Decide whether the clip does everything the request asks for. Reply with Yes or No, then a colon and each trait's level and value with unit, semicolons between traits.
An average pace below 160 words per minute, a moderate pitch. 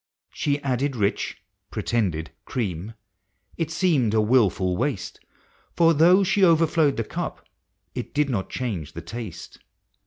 No: slow, 135 wpm; low, 125 Hz